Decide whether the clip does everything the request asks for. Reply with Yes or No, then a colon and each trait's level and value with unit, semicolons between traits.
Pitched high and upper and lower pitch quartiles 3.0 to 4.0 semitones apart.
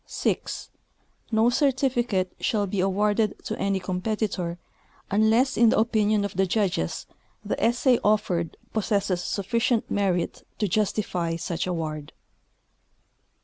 Yes: high, 205 Hz; average, 3.4 semitones